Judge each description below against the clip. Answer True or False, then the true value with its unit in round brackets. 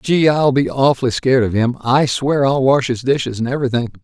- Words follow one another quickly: True (225 wpm)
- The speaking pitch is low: True (130 Hz)